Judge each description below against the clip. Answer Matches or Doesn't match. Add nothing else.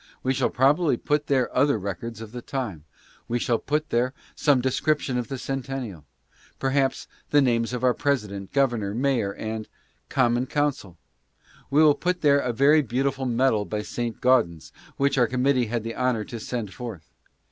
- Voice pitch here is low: Matches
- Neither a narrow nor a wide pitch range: Matches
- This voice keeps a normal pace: Matches